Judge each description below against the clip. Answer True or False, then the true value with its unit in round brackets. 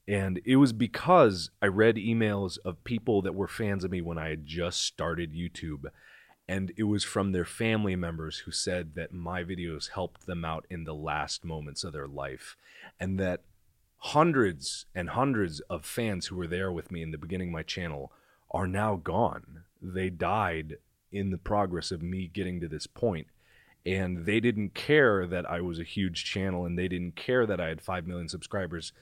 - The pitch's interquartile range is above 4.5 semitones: False (3.2 semitones)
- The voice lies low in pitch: True (90 Hz)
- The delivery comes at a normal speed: True (195 wpm)